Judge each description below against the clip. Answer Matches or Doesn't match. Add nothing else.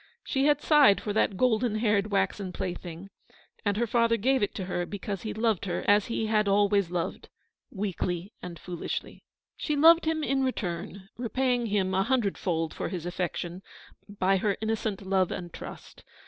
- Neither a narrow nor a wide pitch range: Matches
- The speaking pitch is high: Matches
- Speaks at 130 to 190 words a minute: Matches